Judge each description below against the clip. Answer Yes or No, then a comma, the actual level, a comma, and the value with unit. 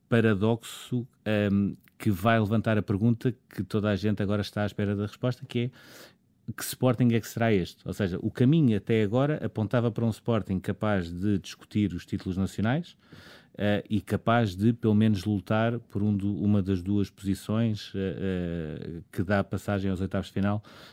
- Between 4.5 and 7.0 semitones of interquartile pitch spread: No, narrow, 2.5 semitones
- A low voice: Yes, low, 105 Hz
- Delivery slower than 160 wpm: No, fast, 185 wpm